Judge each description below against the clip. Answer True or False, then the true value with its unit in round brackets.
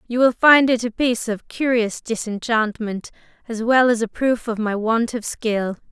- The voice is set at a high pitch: True (230 Hz)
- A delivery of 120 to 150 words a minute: False (195 wpm)